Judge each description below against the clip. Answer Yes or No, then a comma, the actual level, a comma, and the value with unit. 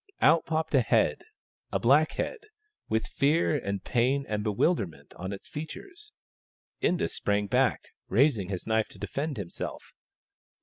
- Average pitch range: No, wide, 7.5 semitones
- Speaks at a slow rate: No, average, 145 wpm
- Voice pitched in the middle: No, low, 125 Hz